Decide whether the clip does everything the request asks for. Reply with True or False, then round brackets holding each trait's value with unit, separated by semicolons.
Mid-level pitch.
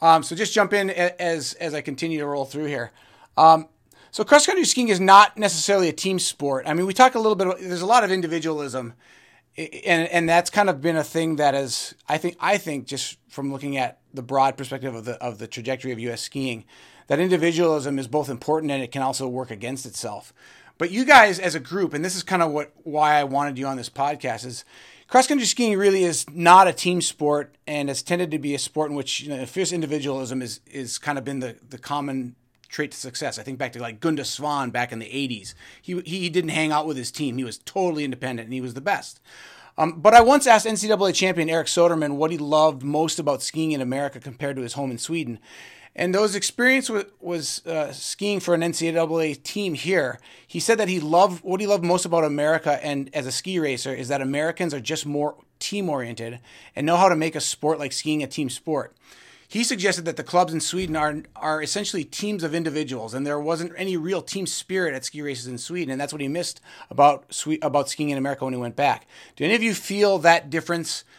True (155 Hz)